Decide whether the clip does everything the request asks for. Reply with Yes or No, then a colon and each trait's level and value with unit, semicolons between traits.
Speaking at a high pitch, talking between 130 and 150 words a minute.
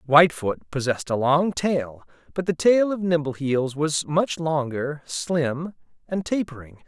No: medium, 150 Hz; average, 140 wpm